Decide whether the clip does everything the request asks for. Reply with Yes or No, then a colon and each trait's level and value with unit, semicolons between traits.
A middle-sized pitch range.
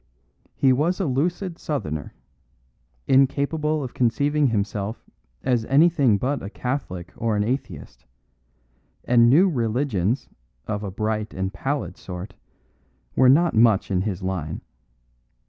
No: wide, 5.9 semitones